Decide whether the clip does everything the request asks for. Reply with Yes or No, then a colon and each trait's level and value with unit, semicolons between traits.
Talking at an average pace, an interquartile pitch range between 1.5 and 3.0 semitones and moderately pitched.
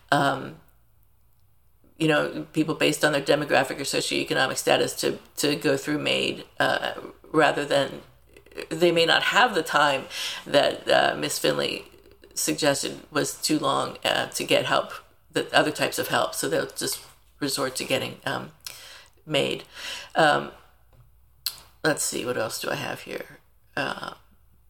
Yes: average, 145 wpm; narrow, 2.5 semitones; medium, 155 Hz